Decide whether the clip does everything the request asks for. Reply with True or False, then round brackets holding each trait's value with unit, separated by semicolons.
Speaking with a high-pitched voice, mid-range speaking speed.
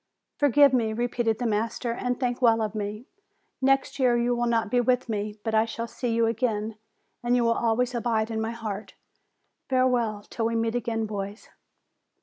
True (230 Hz; 185 wpm)